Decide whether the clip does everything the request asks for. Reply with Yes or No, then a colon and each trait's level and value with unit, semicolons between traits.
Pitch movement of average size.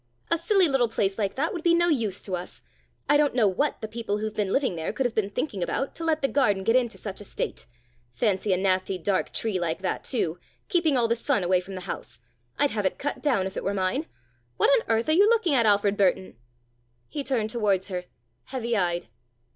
No: wide, 6.3 semitones